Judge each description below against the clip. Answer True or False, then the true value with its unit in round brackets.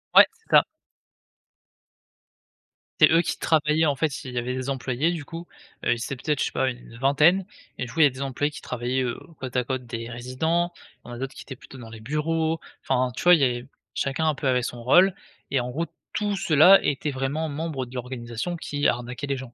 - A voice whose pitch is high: False (135 Hz)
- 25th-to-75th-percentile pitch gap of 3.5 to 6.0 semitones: True (4.1 semitones)